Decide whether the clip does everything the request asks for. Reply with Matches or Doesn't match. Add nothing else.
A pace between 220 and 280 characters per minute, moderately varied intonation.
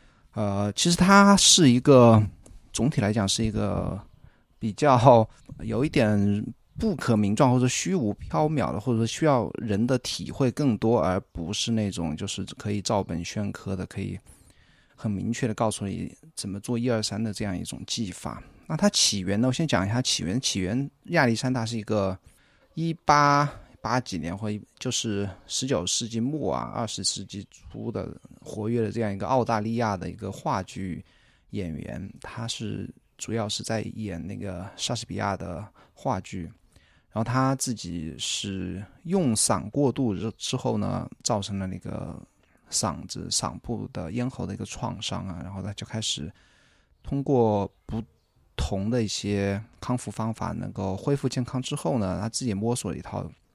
Matches